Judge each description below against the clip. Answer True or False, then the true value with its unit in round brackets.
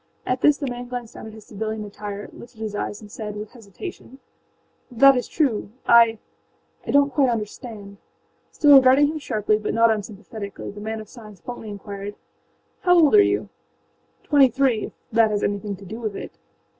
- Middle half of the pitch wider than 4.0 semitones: False (3.6 semitones)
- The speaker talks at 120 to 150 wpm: False (180 wpm)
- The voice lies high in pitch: True (220 Hz)